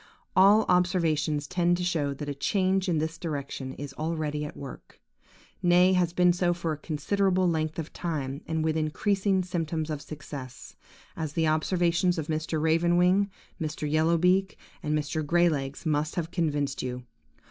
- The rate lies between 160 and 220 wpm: Yes, average, 170 wpm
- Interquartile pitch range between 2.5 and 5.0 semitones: Yes, average, 2.9 semitones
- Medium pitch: Yes, medium, 160 Hz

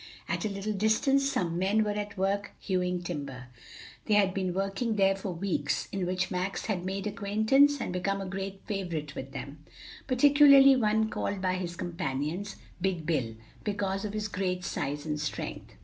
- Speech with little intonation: No, average, 3.0 semitones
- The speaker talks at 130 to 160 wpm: No, average, 175 wpm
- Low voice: No, high, 195 Hz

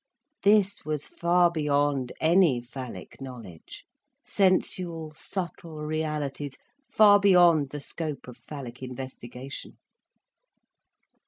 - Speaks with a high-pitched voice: No, medium, 150 Hz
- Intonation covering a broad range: No, average, 4.7 semitones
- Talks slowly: Yes, slow, 90 wpm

